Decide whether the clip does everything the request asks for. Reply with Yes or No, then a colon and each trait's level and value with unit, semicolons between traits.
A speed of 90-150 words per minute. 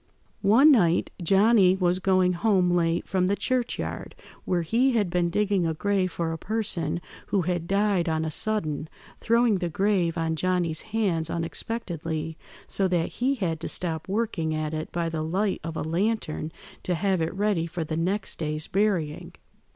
No: average, 175 wpm